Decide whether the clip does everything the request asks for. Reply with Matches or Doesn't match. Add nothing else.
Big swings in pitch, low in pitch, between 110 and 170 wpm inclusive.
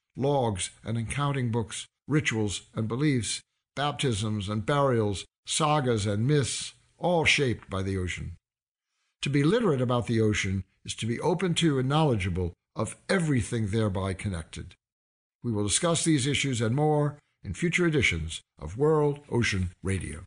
Matches